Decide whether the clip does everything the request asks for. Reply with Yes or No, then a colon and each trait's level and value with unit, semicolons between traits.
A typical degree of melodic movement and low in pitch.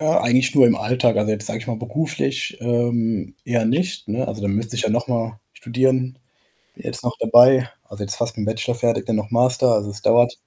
No: narrow, 2.2 semitones; low, 120 Hz